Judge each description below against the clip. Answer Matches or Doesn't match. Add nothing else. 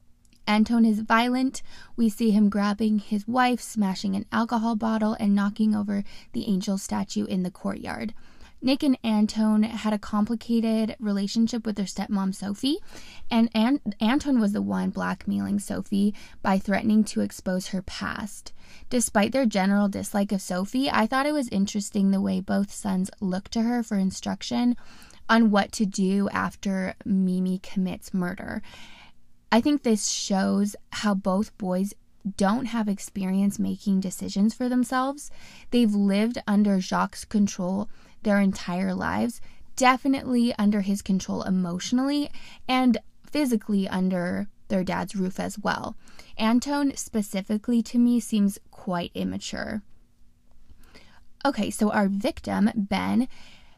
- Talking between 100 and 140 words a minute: Matches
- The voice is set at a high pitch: Matches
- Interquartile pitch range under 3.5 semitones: Matches